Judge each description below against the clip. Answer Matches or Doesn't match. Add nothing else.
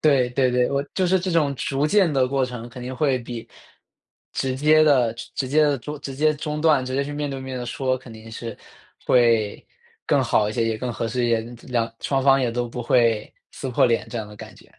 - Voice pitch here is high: Doesn't match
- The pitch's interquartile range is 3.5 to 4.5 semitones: Doesn't match